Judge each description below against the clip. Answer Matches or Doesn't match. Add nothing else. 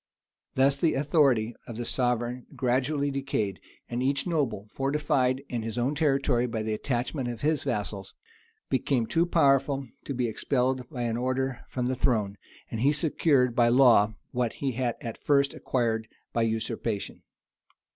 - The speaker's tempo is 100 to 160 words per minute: Matches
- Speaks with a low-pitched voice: Matches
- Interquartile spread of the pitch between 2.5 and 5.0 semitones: Matches